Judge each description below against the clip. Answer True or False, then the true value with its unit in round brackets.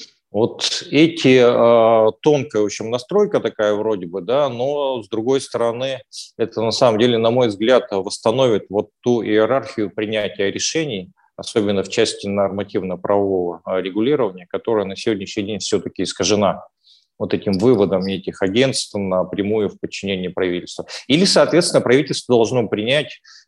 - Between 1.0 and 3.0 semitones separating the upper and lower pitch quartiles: False (4.1 semitones)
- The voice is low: True (110 Hz)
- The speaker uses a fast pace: False (135 wpm)